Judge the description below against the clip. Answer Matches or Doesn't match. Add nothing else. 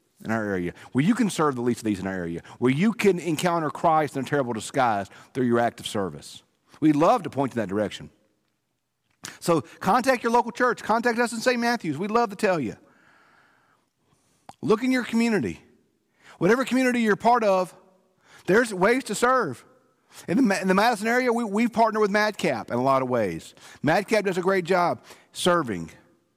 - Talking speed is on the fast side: Doesn't match